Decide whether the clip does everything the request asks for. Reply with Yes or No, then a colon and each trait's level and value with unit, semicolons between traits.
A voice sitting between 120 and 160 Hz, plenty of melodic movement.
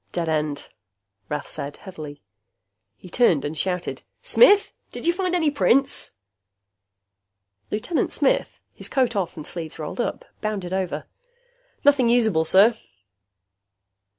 No: high, 190 Hz; wide, 8.5 semitones